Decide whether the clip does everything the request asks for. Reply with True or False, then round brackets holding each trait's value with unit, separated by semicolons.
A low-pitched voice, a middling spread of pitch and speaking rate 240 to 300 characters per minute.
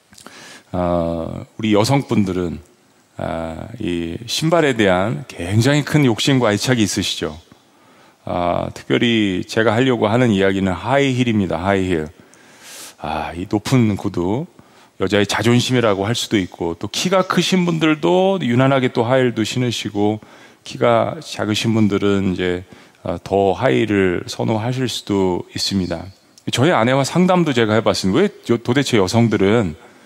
True (110 Hz; 4.7 semitones; 280 characters per minute)